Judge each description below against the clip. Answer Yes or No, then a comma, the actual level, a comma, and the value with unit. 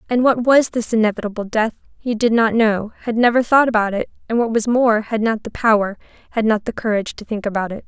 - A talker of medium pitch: No, high, 225 Hz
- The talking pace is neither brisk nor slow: No, fast, 230 wpm